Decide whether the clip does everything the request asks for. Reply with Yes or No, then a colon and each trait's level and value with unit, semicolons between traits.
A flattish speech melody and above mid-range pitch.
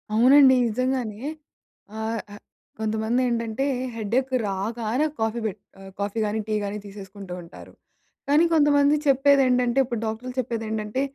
No: average, 3.4 semitones; high, 230 Hz